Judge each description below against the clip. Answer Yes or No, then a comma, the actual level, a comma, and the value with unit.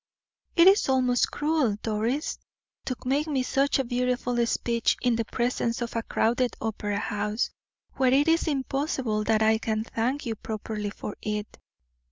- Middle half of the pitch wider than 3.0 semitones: Yes, average, 3.5 semitones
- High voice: Yes, high, 240 Hz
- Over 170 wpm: No, average, 160 wpm